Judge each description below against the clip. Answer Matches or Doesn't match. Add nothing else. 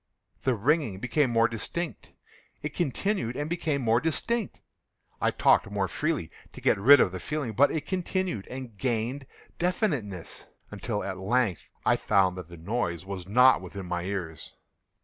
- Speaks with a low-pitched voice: Matches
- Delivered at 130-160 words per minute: Matches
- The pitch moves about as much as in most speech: Doesn't match